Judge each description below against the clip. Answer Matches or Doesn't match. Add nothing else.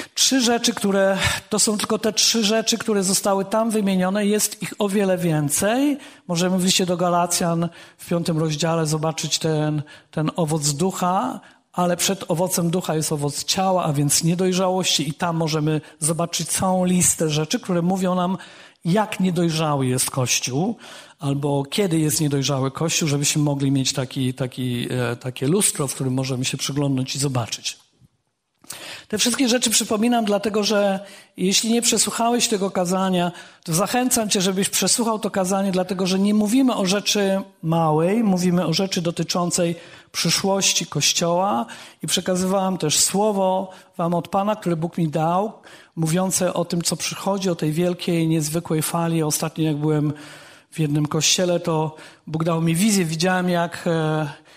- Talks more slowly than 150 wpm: Doesn't match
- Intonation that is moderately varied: Matches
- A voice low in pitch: Doesn't match